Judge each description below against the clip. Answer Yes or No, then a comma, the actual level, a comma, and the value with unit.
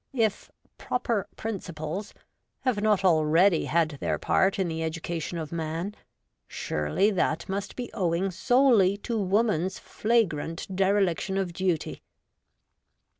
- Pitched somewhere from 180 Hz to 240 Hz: Yes, high, 190 Hz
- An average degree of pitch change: Yes, average, 3.9 semitones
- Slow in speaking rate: Yes, slow, 125 wpm